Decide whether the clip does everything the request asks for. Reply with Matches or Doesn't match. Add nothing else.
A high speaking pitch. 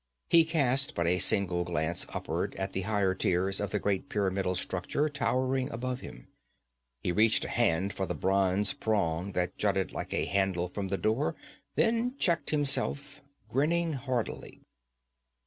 Doesn't match